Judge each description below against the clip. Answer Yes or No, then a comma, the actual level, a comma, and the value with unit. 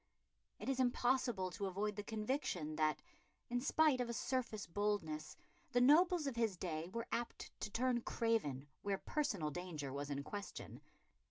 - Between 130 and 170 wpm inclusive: Yes, average, 160 wpm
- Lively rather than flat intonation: Yes, wide, 6.7 semitones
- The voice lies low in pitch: No, high, 210 Hz